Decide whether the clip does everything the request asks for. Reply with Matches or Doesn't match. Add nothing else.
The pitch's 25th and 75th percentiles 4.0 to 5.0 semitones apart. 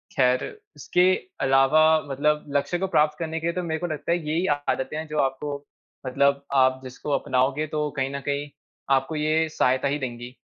Doesn't match